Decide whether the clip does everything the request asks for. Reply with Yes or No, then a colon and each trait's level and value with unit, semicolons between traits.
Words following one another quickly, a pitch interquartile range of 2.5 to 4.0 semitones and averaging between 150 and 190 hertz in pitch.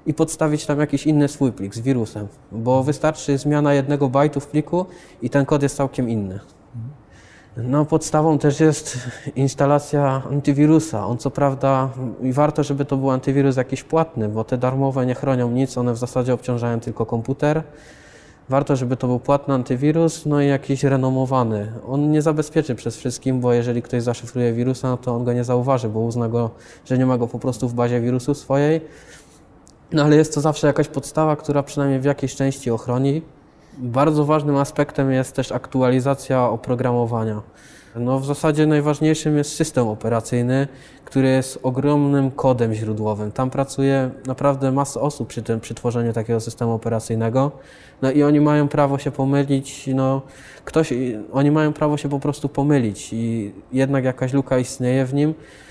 No: fast, 170 wpm; average, 2.9 semitones; low, 135 Hz